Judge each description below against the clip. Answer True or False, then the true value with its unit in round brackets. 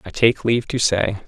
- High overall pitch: False (110 Hz)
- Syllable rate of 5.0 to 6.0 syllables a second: True (5.2 syllables/s)